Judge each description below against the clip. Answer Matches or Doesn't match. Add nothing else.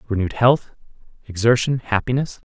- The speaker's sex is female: Doesn't match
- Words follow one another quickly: Doesn't match